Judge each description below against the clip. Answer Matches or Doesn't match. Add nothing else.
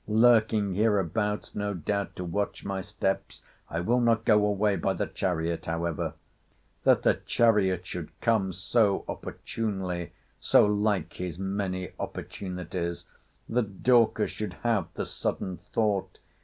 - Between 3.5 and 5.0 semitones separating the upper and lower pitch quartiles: Doesn't match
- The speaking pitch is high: Doesn't match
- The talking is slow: Matches